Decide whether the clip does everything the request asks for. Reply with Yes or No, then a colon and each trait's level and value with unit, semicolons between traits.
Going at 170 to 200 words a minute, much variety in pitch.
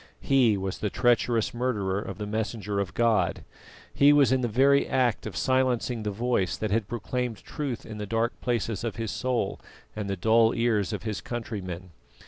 No: average, 185 wpm; average, 3.0 semitones